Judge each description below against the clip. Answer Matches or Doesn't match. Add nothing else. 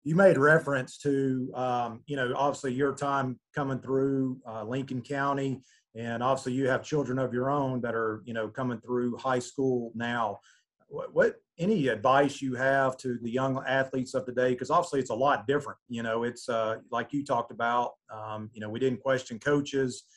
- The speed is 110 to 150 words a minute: Doesn't match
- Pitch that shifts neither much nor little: Doesn't match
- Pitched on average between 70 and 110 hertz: Doesn't match